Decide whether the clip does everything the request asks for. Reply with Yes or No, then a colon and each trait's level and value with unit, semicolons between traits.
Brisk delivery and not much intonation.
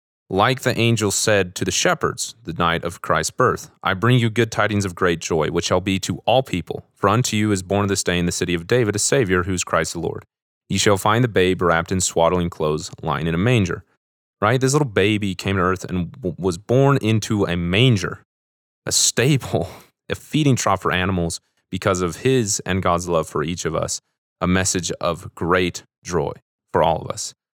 No: fast, 210 wpm; average, 4.2 semitones